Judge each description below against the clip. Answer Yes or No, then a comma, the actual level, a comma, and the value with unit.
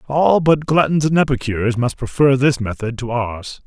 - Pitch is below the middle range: Yes, low, 130 Hz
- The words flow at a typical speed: Yes, average, 180 wpm